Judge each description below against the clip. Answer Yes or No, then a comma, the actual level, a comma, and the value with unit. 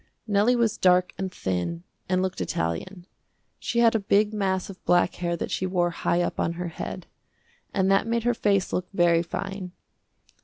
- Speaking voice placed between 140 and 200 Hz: Yes, medium, 185 Hz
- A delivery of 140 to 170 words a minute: No, average, 185 wpm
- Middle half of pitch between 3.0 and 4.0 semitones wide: No, narrow, 2.5 semitones